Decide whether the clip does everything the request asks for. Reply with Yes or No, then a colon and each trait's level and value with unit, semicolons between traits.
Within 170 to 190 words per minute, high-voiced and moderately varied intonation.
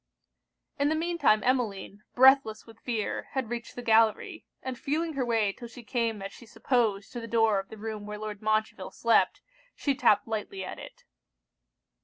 Yes: average, 185 wpm; high, 230 Hz; average, 3.2 semitones